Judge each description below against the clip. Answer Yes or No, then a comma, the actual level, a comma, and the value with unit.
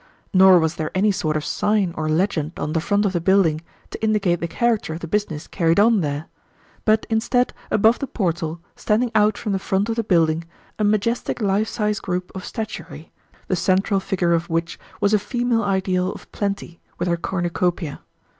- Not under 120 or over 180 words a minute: No, average, 190 wpm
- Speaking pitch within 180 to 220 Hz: Yes, high, 190 Hz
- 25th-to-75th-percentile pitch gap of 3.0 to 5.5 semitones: Yes, average, 3.9 semitones